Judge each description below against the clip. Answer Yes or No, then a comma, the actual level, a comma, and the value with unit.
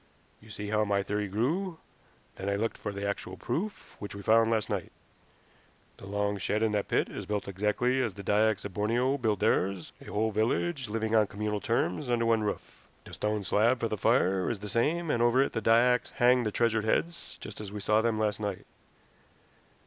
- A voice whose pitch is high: No, low, 110 Hz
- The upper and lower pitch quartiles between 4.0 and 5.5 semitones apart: No, narrow, 2.4 semitones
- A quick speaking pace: Yes, fast, 210 wpm